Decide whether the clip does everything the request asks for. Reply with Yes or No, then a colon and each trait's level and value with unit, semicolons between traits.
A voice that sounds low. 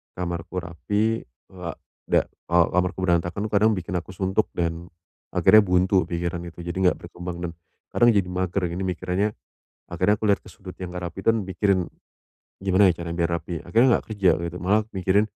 Yes: very low, 90 Hz